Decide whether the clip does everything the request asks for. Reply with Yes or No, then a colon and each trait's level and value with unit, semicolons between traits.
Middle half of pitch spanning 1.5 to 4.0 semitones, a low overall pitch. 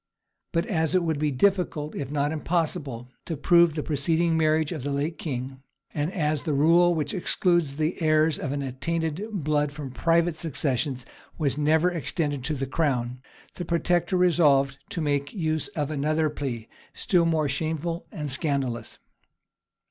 No: average, 2.9 semitones; medium, 155 Hz